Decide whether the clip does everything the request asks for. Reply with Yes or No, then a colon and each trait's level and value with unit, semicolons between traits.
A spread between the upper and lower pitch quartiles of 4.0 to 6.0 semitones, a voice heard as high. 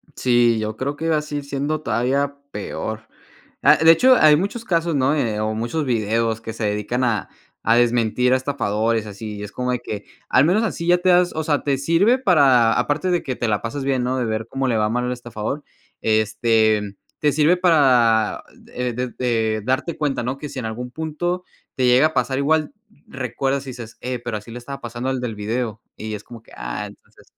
No: average, 4.5 semitones; low, 125 Hz